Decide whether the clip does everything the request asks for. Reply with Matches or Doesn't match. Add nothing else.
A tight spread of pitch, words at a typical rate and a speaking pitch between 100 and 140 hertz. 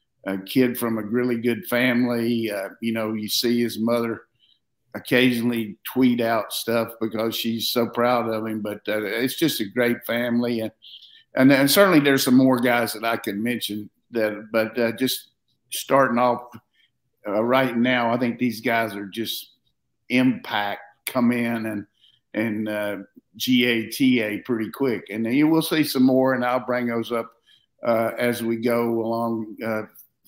Matches